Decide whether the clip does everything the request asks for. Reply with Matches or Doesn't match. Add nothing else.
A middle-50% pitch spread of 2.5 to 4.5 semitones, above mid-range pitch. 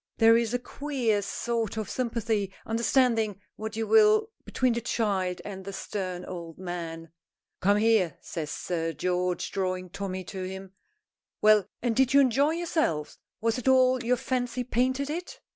Doesn't match